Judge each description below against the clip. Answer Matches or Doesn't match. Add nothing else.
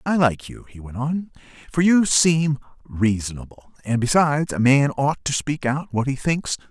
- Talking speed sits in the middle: Matches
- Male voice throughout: Matches